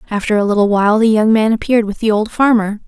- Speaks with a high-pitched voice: Yes, high, 215 Hz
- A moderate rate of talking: No, fast, 250 wpm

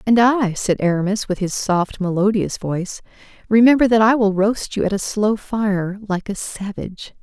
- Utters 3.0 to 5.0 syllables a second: Yes, 4.8 syllables/s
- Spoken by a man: No, female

